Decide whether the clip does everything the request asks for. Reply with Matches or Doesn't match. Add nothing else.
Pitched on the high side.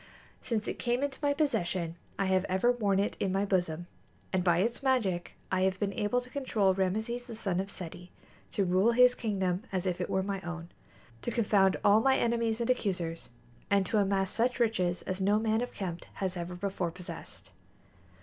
Matches